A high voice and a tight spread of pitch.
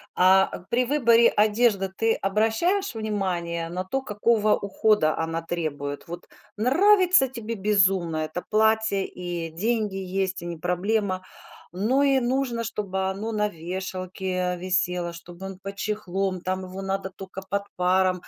No: high, 195 Hz; average, 3.5 semitones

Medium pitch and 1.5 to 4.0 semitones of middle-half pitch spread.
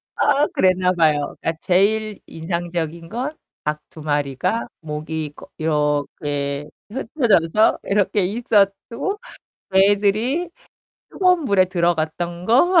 No: medium, 180 Hz; wide, 5.6 semitones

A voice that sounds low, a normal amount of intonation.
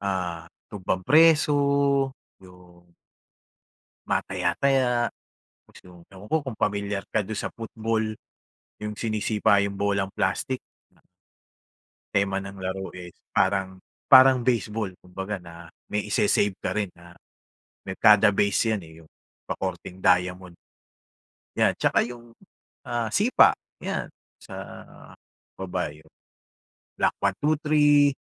Yes: low, 100 Hz; average, 3.4 semitones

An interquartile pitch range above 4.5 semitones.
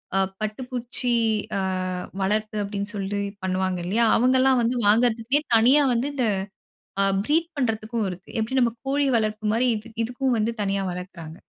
No: average, 3.6 semitones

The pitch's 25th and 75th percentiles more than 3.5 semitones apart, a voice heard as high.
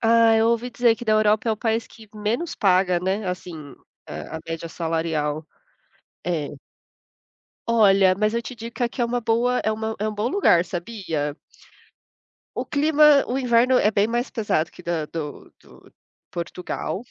Yes: average, 5.1 semitones; high, 215 Hz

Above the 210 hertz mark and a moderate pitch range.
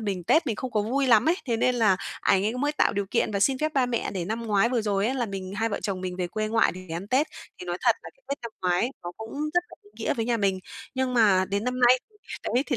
Yes: high, 225 Hz; average, 4.3 semitones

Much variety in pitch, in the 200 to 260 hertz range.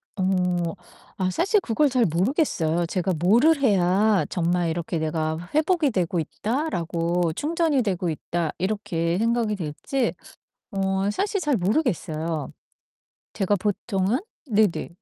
No: wide, 5.9 semitones; high, 190 Hz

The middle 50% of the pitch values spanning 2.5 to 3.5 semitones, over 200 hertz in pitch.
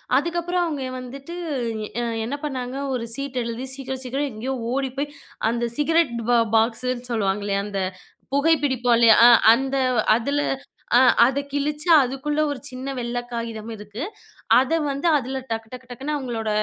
Yes: average, 3.0 semitones; very high, 255 Hz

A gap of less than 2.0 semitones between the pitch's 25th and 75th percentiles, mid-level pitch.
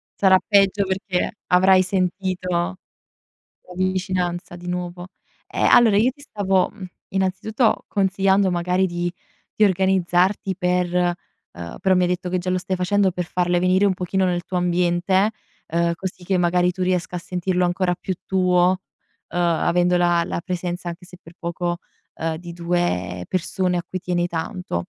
Yes: narrow, 1.3 semitones; medium, 180 Hz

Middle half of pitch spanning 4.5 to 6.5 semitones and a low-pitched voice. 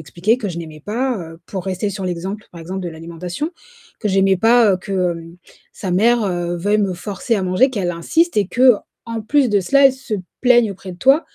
No: average, 4.9 semitones; high, 200 Hz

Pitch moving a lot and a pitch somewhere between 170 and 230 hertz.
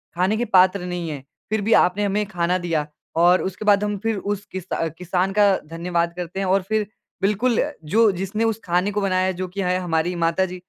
No: narrow, 2.5 semitones; medium, 185 Hz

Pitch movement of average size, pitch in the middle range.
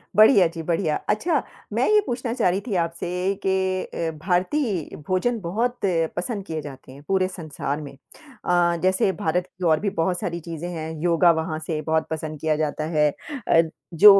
Yes: average, 3.7 semitones; medium, 175 Hz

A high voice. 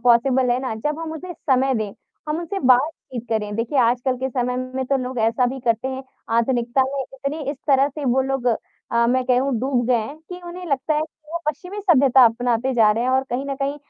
Yes: very high, 260 Hz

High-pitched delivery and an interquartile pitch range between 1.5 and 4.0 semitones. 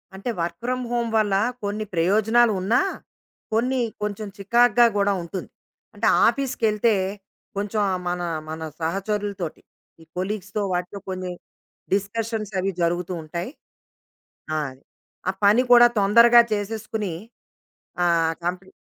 Yes: high, 205 Hz; average, 3.6 semitones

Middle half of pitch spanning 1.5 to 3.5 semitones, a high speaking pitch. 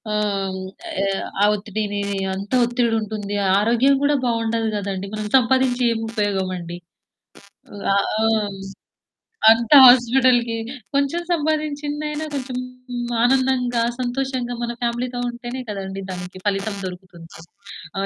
No: average, 4.2 semitones; high, 235 Hz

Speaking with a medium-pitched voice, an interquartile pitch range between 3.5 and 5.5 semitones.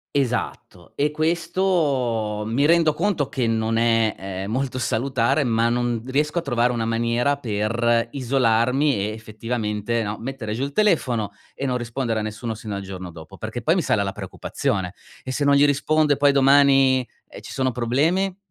No: low, 120 Hz; average, 4.0 semitones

